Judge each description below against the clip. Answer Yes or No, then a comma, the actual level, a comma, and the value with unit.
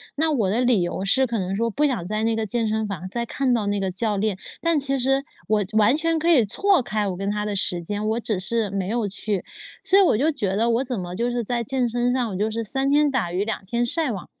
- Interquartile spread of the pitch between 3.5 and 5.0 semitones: Yes, average, 4.2 semitones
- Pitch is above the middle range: Yes, high, 225 Hz